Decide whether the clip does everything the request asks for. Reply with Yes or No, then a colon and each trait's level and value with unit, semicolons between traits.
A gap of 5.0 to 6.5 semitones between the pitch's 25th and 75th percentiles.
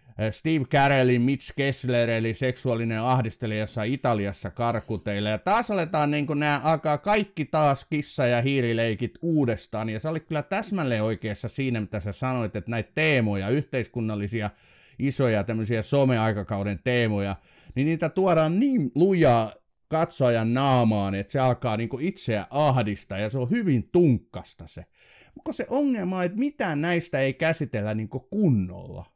Yes: wide, 5.6 semitones